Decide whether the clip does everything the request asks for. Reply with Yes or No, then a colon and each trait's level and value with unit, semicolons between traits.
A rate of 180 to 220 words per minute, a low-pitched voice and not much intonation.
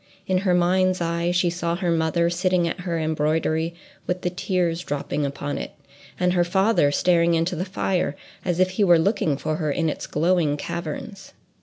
No: average, 185 wpm; medium, 170 Hz; narrow, 2.1 semitones